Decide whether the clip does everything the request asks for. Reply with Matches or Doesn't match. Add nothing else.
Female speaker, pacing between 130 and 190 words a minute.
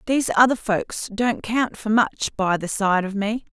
Doesn't match